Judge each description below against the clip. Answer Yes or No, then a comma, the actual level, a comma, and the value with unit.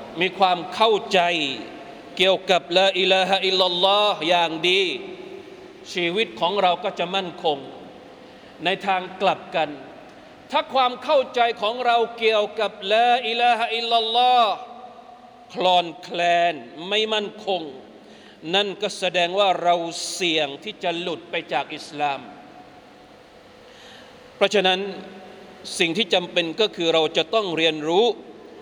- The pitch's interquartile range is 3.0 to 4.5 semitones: No, average, 5.1 semitones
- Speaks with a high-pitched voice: Yes, high, 195 Hz